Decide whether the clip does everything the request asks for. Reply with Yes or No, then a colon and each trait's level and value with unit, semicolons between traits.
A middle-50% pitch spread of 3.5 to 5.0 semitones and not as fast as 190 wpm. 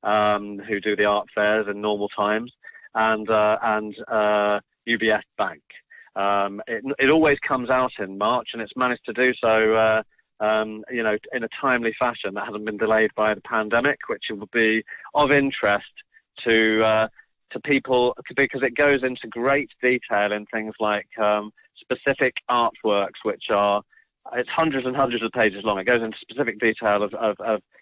No: average, 3.1 semitones; average, 175 wpm